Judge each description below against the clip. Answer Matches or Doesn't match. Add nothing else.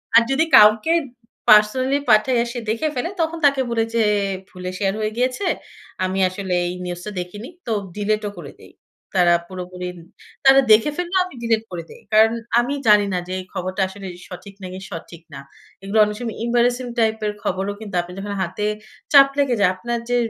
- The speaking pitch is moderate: Doesn't match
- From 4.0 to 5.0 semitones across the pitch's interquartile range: Matches